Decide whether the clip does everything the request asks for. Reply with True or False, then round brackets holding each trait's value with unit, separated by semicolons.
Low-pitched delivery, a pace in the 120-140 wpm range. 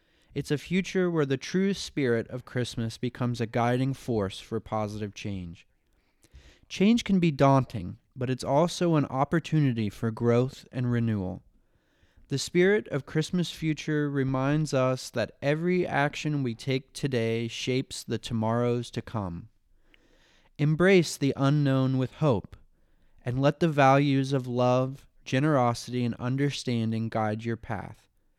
True (130 Hz; 135 wpm)